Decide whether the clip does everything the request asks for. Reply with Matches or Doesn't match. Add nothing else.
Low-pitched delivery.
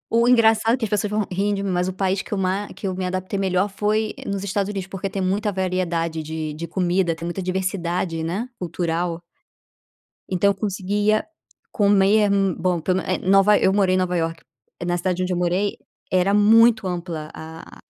Doesn't match